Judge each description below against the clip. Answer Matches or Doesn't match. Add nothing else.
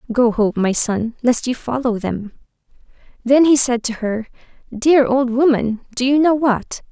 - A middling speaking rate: Matches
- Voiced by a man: Doesn't match